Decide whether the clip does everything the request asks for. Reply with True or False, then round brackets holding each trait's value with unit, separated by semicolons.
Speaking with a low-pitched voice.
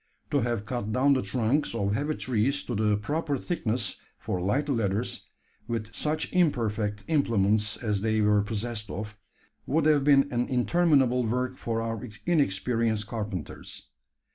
True (115 Hz)